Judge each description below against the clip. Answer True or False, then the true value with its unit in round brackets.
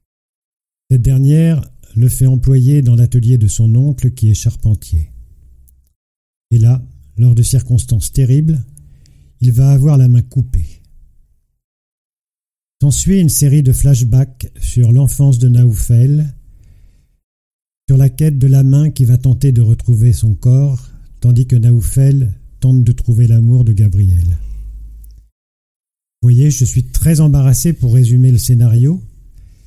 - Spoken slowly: True (135 wpm)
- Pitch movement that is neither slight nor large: True (4.7 semitones)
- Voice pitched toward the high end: False (120 Hz)